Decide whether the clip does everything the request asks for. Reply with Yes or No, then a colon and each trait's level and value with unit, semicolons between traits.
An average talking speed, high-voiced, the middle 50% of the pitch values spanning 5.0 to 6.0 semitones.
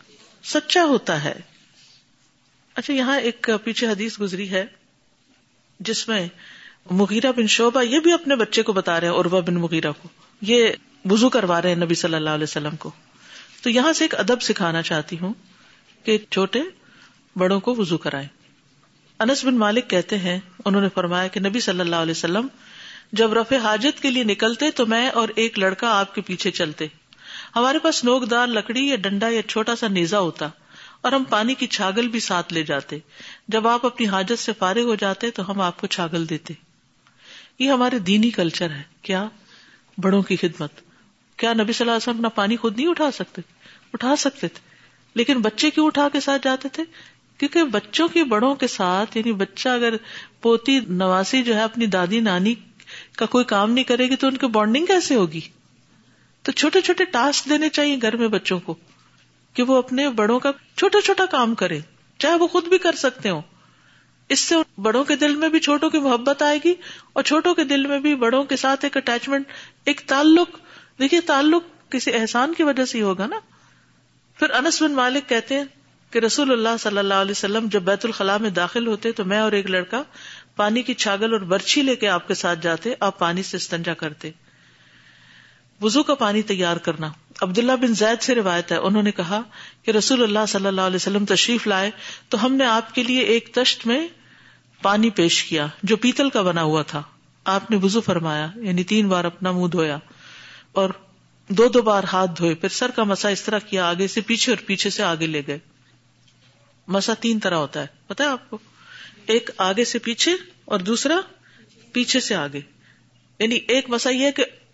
No: fast, 195 wpm; high, 220 Hz; wide, 5.5 semitones